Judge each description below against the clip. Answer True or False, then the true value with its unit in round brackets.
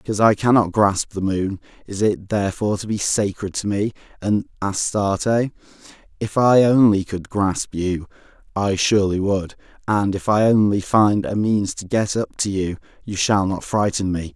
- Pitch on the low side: True (100 Hz)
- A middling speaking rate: True (175 wpm)